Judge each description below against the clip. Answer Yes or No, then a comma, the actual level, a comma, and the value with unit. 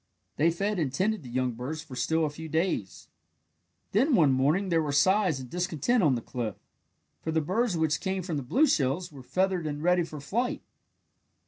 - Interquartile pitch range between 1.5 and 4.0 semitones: No, average, 5.1 semitones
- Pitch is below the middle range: No, medium, 160 Hz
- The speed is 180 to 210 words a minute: Yes, average, 200 wpm